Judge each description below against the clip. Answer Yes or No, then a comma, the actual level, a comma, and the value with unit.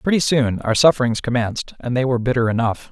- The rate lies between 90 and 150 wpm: No, fast, 205 wpm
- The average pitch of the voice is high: No, low, 125 Hz